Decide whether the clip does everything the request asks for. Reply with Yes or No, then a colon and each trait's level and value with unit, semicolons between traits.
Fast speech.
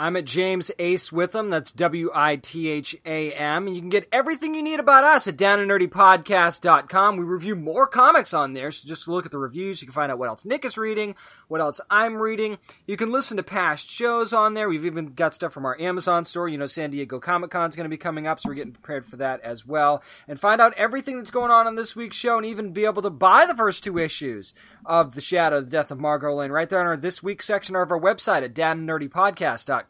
Yes: fast, 255 wpm